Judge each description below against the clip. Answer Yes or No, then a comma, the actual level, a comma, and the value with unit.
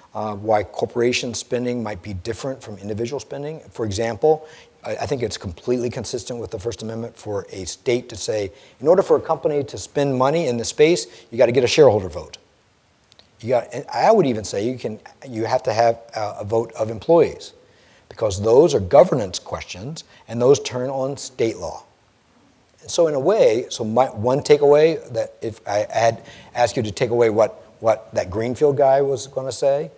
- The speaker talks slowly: No, average, 195 wpm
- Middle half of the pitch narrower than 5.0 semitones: Yes, average, 4.0 semitones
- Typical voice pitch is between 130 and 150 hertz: No, low, 120 Hz